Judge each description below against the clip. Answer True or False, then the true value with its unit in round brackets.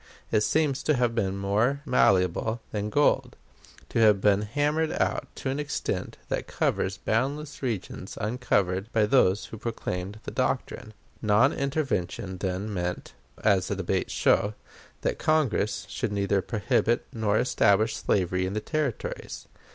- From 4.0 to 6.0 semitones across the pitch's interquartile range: True (4.5 semitones)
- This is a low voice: True (110 Hz)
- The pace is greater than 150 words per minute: False (145 wpm)